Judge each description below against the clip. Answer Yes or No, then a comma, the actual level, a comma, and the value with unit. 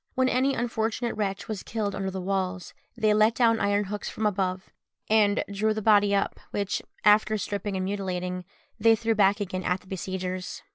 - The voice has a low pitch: No, high, 205 Hz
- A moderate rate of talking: Yes, average, 185 wpm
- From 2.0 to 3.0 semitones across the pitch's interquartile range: Yes, narrow, 2.4 semitones